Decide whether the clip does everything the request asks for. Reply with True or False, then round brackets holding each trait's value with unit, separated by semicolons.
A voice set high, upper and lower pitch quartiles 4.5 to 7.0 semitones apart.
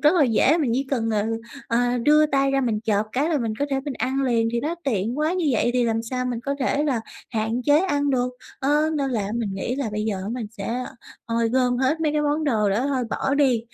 False (250 Hz; 3.9 semitones)